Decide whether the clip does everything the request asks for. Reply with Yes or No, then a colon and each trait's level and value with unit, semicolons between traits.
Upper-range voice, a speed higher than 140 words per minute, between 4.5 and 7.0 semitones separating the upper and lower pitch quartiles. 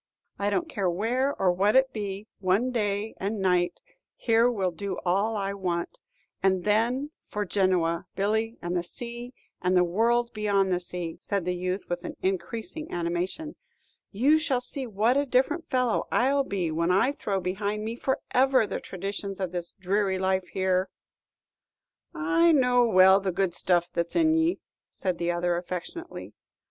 Yes: high, 200 Hz; average, 165 wpm; average, 5.1 semitones